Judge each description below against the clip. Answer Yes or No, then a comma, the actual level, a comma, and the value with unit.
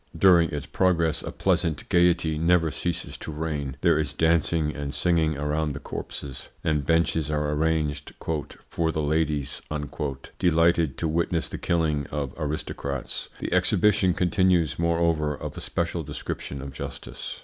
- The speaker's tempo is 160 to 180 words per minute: No, average, 145 wpm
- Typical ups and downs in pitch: No, narrow, 2.2 semitones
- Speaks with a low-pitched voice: Yes, very low, 80 Hz